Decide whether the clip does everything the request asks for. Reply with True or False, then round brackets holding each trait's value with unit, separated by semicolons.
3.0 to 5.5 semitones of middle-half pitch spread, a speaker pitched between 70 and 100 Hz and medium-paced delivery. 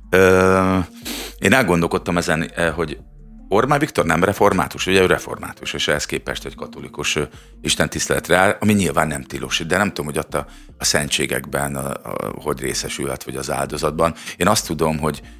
False (4.2 semitones; 80 Hz; 165 wpm)